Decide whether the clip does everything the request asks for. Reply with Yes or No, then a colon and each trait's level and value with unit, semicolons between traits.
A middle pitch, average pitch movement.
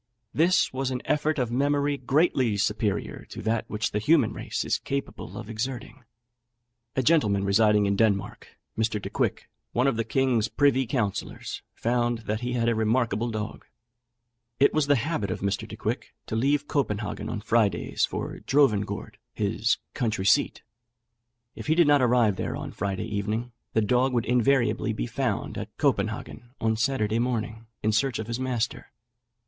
No: low, 115 Hz; average, 3.7 semitones